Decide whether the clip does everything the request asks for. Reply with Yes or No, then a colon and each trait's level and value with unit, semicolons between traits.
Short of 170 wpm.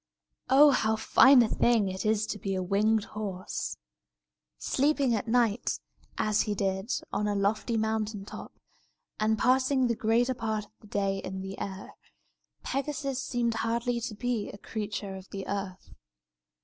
Yes: average, 160 wpm